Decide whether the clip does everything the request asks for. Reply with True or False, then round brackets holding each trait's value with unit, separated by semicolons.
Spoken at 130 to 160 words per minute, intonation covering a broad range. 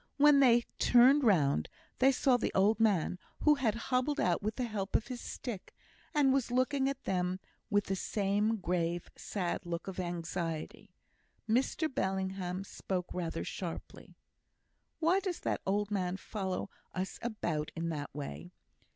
True (150 wpm; 5.7 semitones)